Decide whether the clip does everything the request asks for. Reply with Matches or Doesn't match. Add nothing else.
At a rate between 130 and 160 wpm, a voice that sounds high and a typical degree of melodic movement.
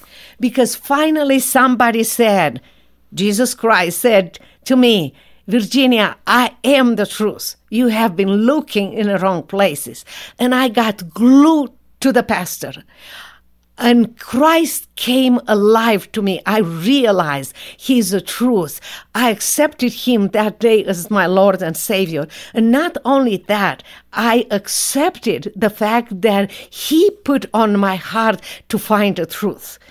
Matches